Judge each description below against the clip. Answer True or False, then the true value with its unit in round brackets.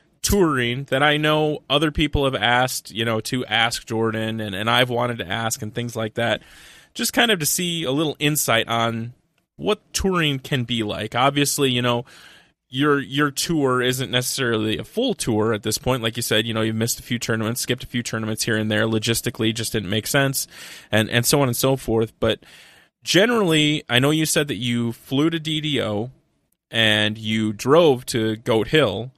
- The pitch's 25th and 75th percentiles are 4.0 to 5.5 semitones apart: True (4.4 semitones)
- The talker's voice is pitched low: True (120 Hz)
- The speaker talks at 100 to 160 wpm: False (200 wpm)